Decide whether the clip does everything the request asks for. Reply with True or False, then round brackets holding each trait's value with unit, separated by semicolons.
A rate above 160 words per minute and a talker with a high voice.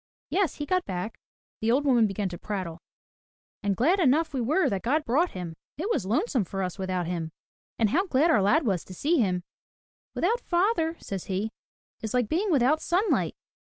True (195 wpm; 245 Hz)